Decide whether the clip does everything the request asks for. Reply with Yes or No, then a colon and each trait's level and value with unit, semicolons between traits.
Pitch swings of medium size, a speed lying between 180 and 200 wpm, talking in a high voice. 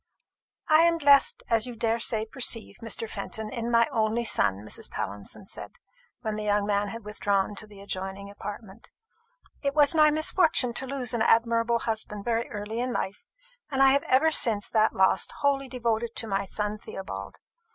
Yes: average, 3.7 semitones; average, 185 wpm; high, 225 Hz